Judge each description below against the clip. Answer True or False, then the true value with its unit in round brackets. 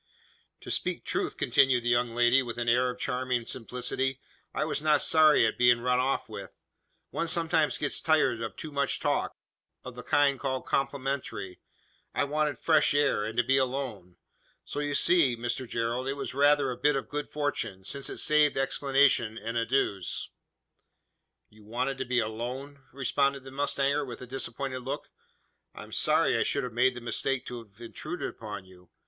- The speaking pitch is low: True (130 Hz)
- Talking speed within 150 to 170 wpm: False (180 wpm)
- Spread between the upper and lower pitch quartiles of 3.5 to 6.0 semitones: False (2.9 semitones)